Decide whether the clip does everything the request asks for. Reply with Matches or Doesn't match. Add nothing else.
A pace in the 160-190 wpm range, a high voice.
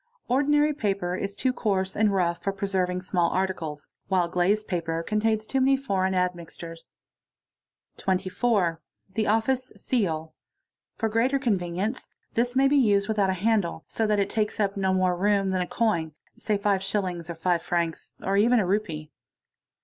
Matches